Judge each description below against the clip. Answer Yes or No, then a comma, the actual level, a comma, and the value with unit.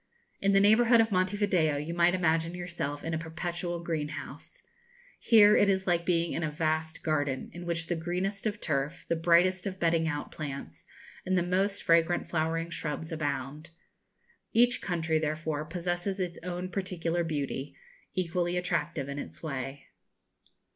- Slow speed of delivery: No, average, 160 wpm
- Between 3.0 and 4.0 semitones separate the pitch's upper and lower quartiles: No, narrow, 2.6 semitones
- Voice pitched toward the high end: No, medium, 170 Hz